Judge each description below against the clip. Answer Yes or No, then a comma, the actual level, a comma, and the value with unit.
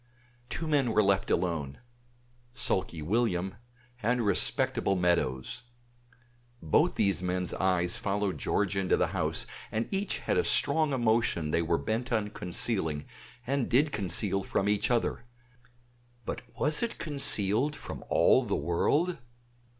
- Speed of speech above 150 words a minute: No, slow, 135 wpm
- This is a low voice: Yes, low, 100 Hz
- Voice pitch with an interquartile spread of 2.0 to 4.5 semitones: No, wide, 5.4 semitones